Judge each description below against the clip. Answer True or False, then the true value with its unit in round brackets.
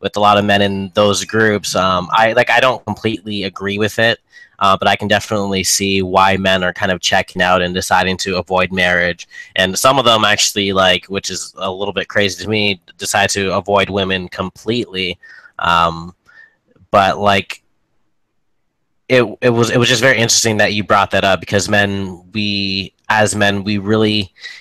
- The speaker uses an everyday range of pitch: False (2.1 semitones)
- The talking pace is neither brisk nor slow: True (190 wpm)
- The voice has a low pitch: True (100 Hz)